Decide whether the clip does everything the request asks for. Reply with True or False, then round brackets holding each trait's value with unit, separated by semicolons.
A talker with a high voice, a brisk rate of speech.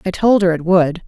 False (180 Hz; 280 wpm)